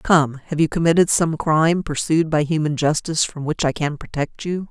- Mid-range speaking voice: Yes, medium, 160 Hz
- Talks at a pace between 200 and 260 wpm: Yes, fast, 205 wpm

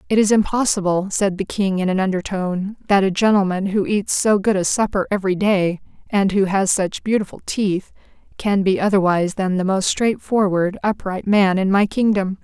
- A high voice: Yes, high, 195 Hz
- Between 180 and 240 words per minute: Yes, average, 185 wpm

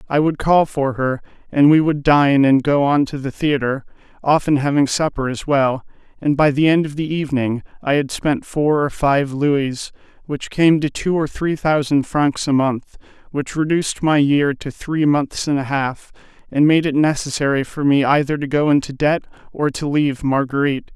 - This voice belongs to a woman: No, male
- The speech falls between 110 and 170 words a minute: No, average, 200 wpm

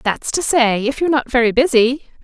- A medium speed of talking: No, fast, 215 wpm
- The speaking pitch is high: Yes, very high, 255 Hz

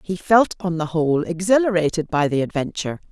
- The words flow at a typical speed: Yes, average, 175 wpm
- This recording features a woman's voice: Yes, female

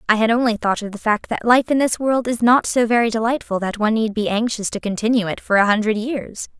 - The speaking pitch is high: Yes, high, 225 Hz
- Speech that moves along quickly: Yes, fast, 265 wpm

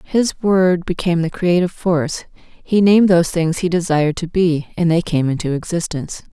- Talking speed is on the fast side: No, average, 180 wpm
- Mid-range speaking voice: Yes, medium, 170 Hz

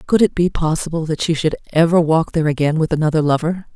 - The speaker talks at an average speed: No, fast, 225 wpm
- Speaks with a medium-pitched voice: Yes, medium, 160 Hz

